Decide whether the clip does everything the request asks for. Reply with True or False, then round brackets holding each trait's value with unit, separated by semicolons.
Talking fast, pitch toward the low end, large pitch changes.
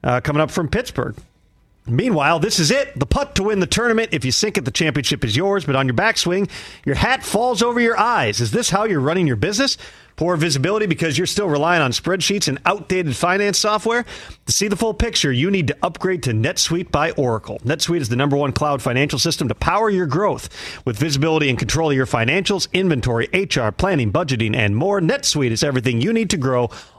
False (215 wpm; 160 Hz; 7.1 semitones)